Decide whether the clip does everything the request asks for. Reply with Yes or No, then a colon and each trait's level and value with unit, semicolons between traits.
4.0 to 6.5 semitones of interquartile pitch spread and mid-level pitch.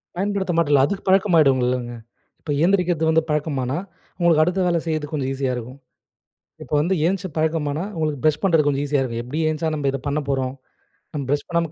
No: average, 3.5 semitones; medium, 155 Hz